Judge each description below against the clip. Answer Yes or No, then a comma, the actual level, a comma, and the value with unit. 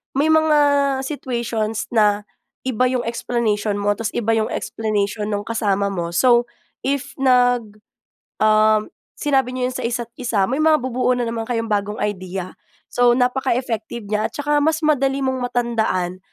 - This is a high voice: Yes, high, 235 Hz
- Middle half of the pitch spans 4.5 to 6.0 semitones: No, average, 3.4 semitones